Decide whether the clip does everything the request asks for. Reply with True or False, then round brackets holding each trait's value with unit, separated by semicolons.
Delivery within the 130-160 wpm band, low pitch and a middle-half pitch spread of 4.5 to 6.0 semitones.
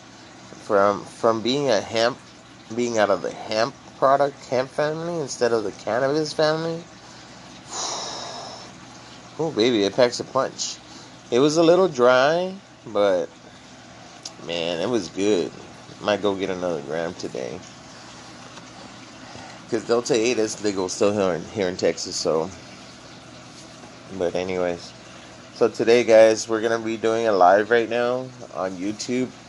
True (140 wpm; 110 Hz; 5.3 semitones)